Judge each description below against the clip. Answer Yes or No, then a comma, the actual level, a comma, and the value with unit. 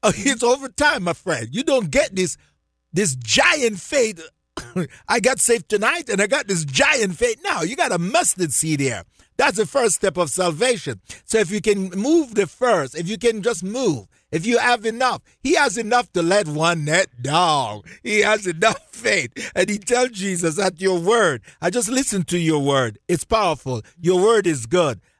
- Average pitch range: No, wide, 6.3 semitones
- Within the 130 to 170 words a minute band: No, average, 195 wpm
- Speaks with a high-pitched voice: Yes, high, 195 Hz